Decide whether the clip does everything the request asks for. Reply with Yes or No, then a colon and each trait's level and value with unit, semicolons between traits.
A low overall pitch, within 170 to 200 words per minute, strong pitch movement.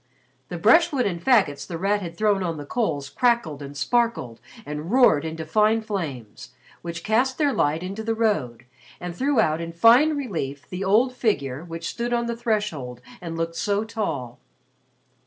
No: high, 190 Hz; average, 175 wpm; wide, 6.6 semitones